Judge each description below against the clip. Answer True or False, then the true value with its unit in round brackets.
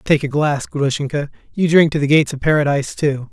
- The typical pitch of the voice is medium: True (145 Hz)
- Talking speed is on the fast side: True (215 wpm)